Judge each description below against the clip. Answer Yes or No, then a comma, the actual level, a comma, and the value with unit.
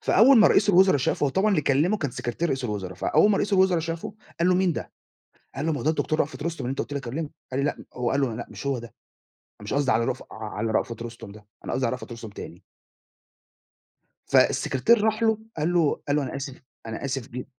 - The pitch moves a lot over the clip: Yes, wide, 6.3 semitones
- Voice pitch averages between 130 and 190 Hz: Yes, medium, 140 Hz